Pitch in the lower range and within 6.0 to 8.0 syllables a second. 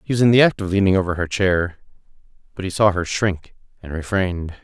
Yes: very low, 95 Hz; 6.1 syllables/s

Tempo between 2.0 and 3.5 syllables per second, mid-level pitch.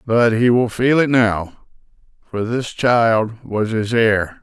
No: 3.4 syllables/s; low, 115 Hz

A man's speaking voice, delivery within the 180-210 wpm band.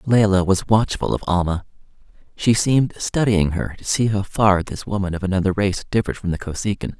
Yes: male; average, 190 wpm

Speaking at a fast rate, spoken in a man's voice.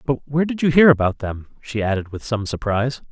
Yes: fast, 230 wpm; male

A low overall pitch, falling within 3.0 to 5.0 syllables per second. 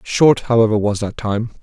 Yes: low, 110 Hz; 4.9 syllables/s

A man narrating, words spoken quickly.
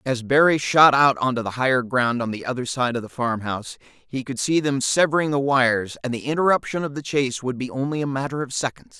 Yes: male; fast, 235 wpm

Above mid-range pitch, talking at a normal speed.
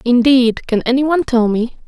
Yes: very high, 250 Hz; average, 160 wpm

